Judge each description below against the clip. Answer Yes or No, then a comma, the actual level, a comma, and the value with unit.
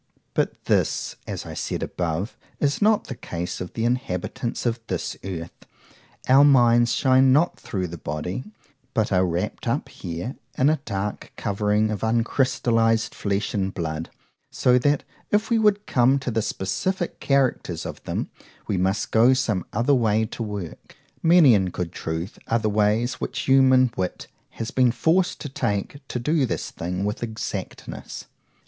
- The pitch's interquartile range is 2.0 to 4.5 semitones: No, average, 5.3 semitones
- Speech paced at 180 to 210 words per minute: No, average, 160 wpm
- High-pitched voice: No, low, 115 Hz